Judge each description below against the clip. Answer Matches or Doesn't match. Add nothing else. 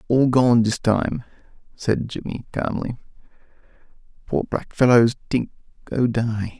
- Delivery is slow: Matches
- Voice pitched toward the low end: Matches